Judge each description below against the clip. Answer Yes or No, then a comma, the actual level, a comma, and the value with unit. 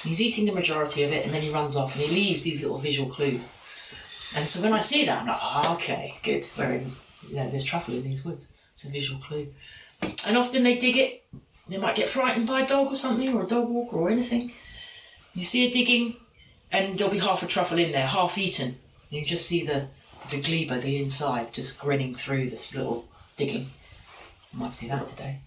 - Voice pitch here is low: No, medium, 160 Hz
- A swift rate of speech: Yes, fast, 225 wpm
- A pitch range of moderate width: No, wide, 8.8 semitones